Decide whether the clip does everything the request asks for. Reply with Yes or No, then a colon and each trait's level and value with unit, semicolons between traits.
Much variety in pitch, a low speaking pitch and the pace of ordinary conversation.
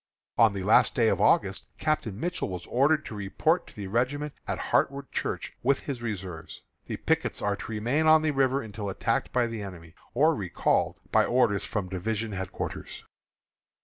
Yes: wide, 5.8 semitones; low, 115 Hz; average, 180 wpm